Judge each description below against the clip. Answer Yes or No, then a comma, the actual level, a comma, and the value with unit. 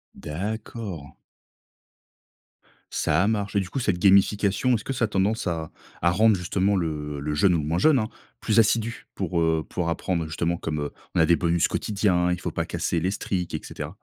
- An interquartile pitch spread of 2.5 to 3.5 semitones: No, average, 4.1 semitones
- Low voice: Yes, very low, 90 Hz